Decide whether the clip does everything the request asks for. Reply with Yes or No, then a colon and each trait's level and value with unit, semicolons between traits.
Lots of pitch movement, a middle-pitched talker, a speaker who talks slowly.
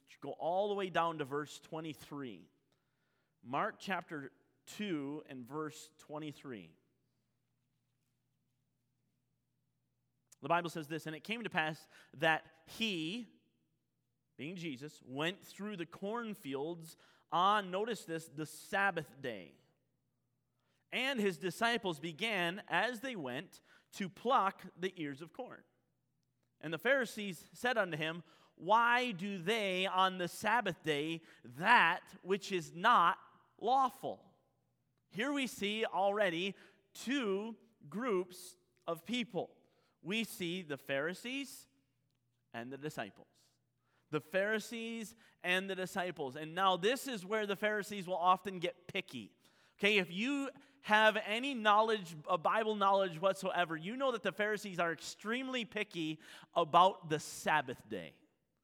Yes: wide, 5.7 semitones; medium, 175 Hz; slow, 125 wpm